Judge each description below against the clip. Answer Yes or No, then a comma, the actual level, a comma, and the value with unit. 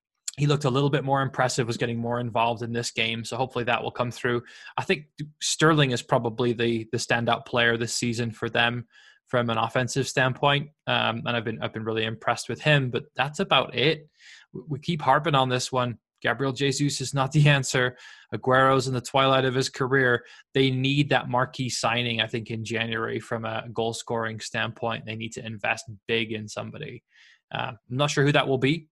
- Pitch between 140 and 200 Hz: No, low, 125 Hz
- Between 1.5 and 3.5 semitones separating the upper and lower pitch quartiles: Yes, average, 2.7 semitones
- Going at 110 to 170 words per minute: No, fast, 205 wpm